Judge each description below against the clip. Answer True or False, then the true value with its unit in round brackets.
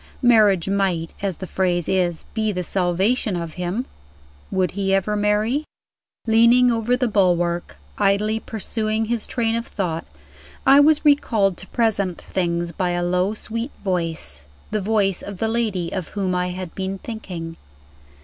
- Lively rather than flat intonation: False (3.8 semitones)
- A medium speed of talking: True (155 wpm)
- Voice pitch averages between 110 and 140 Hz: False (195 Hz)